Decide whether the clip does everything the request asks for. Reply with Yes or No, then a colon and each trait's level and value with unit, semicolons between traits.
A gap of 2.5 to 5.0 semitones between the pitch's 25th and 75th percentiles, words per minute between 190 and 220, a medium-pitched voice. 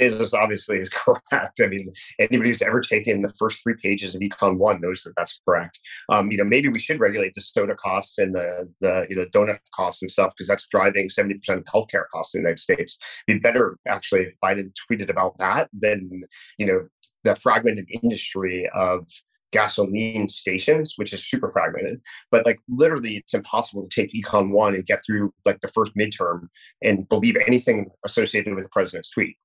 No: average, 2.8 semitones; average, 200 wpm; low, 100 Hz